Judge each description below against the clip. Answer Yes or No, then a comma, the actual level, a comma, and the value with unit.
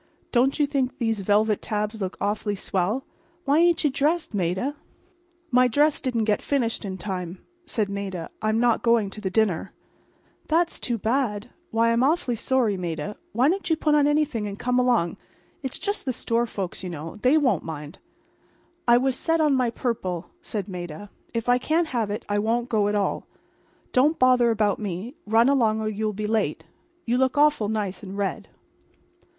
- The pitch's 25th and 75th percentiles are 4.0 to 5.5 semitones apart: Yes, average, 4.4 semitones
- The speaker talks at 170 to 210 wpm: Yes, average, 185 wpm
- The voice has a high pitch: Yes, high, 225 Hz